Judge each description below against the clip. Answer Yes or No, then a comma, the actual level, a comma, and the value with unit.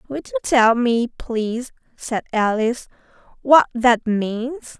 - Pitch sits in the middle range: No, high, 240 Hz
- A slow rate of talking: Yes, slow, 125 wpm